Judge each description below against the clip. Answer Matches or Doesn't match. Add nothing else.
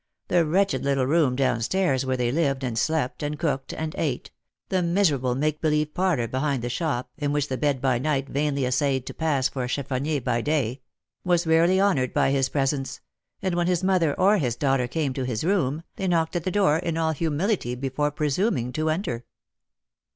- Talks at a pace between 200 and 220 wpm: Matches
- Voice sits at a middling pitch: Matches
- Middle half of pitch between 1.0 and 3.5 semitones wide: Doesn't match